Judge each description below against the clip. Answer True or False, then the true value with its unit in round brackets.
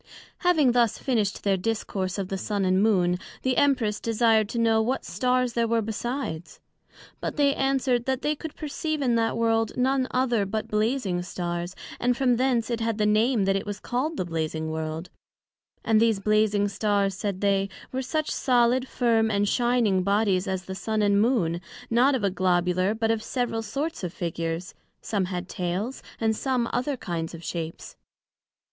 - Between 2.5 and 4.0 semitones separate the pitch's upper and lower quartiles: False (4.5 semitones)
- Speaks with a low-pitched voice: False (220 Hz)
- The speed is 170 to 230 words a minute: True (180 wpm)